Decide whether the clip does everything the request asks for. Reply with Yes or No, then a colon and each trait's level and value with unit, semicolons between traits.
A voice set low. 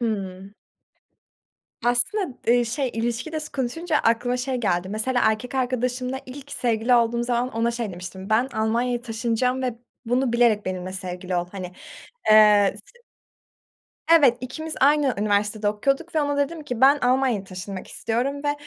No: high, 240 Hz